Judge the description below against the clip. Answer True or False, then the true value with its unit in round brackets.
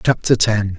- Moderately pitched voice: False (110 Hz)